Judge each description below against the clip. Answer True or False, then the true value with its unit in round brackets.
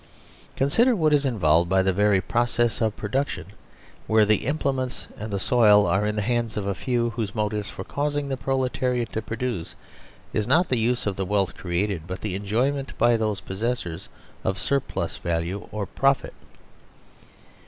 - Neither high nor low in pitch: False (110 Hz)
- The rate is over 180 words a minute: False (175 wpm)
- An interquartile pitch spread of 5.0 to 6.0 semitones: False (4.4 semitones)